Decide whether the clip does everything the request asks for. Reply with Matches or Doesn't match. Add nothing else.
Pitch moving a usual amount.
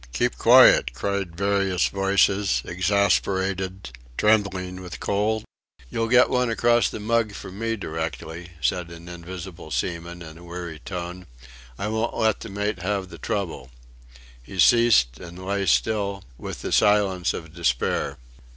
Matches